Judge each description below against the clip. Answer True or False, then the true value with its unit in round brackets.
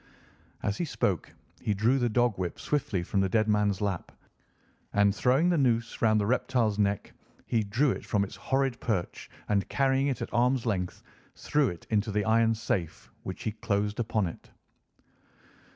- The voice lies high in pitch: False (110 Hz)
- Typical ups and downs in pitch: True (3.7 semitones)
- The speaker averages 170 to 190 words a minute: True (175 wpm)